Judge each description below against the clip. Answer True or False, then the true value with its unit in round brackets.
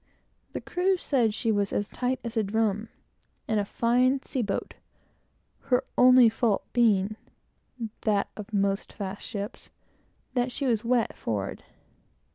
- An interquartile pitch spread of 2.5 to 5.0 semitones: True (3.4 semitones)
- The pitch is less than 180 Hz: False (225 Hz)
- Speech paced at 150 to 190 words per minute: False (140 wpm)